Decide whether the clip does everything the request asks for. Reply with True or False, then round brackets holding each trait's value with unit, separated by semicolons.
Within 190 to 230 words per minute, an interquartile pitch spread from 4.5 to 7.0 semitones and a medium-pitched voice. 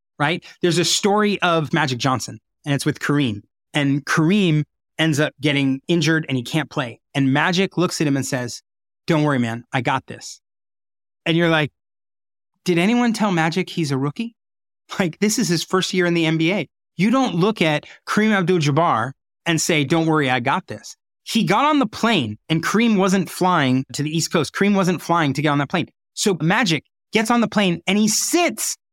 True (200 wpm; 5.3 semitones; 165 Hz)